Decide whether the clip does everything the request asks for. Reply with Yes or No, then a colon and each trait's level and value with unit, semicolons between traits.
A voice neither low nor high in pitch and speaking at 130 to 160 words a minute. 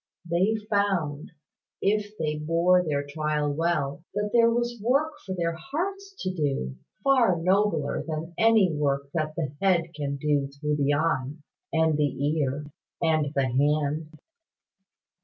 Yes: medium, 160 Hz; average, 140 wpm